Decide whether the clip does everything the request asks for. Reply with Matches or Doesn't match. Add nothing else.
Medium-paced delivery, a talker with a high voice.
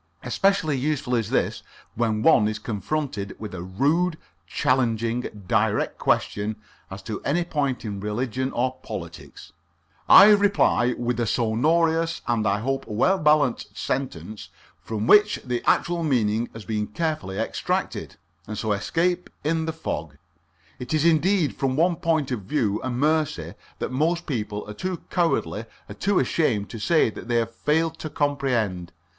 Doesn't match